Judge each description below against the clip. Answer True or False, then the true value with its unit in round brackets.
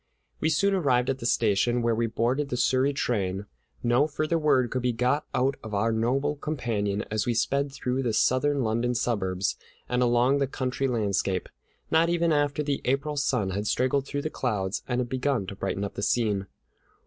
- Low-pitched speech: True (125 Hz)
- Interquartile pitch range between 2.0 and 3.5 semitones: False (4.0 semitones)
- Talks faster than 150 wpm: True (190 wpm)